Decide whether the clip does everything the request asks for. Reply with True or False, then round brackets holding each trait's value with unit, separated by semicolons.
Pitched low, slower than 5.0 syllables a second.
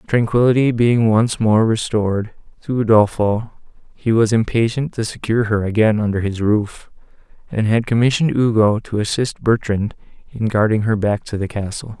False (110 Hz; 5.1 syllables/s)